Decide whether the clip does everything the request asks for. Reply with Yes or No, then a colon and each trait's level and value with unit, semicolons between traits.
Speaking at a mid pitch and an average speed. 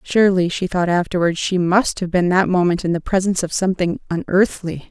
Yes: medium, 180 Hz; average, 195 wpm